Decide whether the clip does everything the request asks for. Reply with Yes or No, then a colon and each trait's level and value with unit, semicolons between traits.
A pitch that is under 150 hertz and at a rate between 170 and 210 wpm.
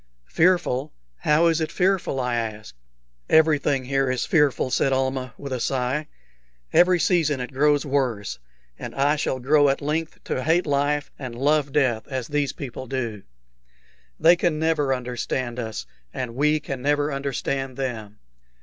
No: medium, 140 Hz; average, 155 wpm